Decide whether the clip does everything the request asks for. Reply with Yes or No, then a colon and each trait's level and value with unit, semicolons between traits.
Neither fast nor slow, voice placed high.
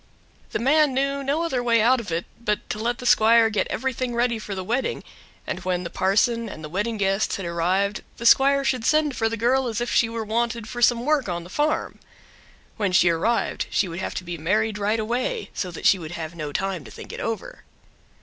No: fast, 230 wpm; high, 225 Hz